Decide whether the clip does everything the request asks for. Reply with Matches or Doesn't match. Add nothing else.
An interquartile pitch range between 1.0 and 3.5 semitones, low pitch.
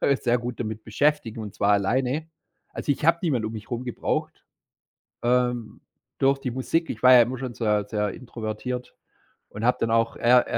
Matches